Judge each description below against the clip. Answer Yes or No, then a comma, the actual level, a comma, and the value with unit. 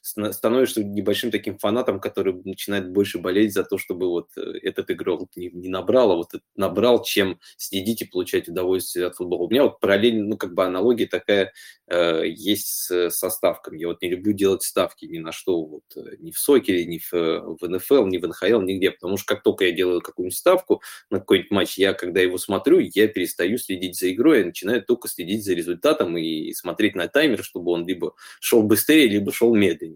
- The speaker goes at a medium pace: No, fast, 200 wpm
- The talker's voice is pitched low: Yes, low, 100 Hz